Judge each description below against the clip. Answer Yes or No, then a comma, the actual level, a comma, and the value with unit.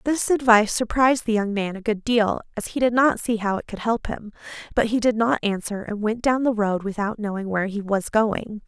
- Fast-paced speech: Yes, fast, 240 wpm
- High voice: Yes, high, 220 Hz